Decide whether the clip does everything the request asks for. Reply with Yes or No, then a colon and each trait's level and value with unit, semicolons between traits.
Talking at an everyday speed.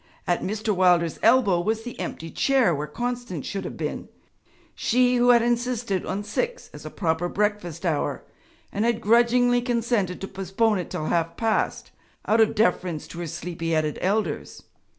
Yes: average, 170 wpm